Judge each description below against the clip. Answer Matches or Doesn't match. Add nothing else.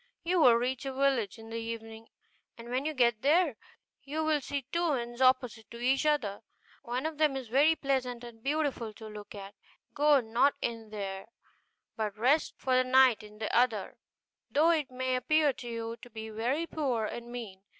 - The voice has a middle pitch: Doesn't match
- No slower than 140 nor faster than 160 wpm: Doesn't match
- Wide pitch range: Doesn't match